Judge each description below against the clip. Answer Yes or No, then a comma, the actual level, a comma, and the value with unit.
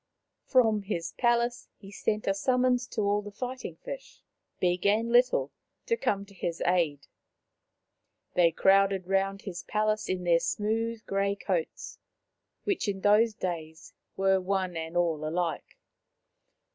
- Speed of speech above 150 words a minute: No, slow, 135 wpm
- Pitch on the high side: Yes, high, 195 Hz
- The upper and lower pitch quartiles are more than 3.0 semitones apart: Yes, average, 3.9 semitones